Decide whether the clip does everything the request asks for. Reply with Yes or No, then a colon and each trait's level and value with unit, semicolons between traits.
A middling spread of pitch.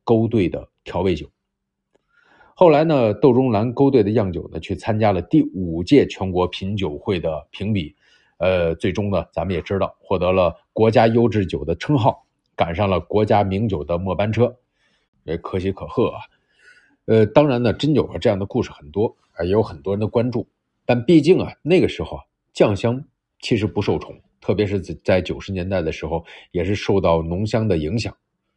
Yes: average, 4.9 semitones